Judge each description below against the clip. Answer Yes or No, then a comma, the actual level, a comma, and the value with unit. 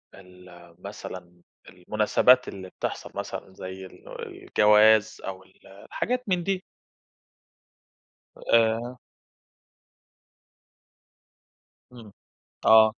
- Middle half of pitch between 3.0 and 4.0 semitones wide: Yes, average, 3.5 semitones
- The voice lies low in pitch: Yes, low, 105 Hz